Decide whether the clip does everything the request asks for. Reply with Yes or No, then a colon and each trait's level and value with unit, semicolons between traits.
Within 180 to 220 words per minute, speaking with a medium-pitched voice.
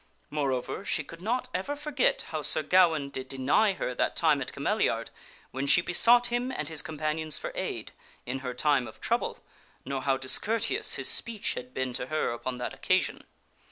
Yes: average, 190 wpm; medium, 155 Hz